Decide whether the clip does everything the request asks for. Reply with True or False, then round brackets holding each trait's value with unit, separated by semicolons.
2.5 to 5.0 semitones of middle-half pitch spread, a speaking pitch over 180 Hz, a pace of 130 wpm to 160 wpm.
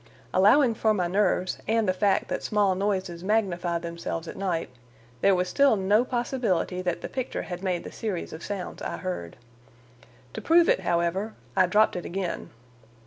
False (3.3 semitones; 190 Hz; 175 wpm)